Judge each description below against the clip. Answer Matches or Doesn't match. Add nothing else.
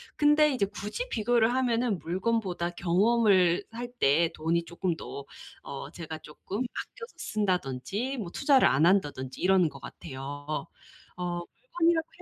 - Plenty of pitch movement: Matches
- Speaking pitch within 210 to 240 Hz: Doesn't match